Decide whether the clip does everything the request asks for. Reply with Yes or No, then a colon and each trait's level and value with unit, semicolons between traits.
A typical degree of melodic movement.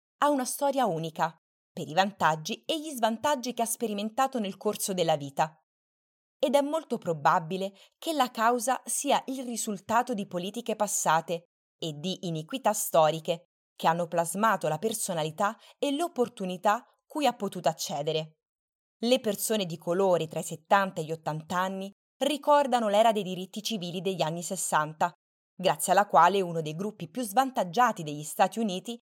No: wide, 5.7 semitones